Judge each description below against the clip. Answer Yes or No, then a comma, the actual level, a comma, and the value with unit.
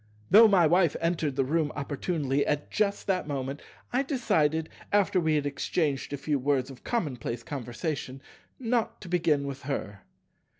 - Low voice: No, medium, 150 Hz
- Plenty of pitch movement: No, average, 4.4 semitones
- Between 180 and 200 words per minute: No, average, 160 wpm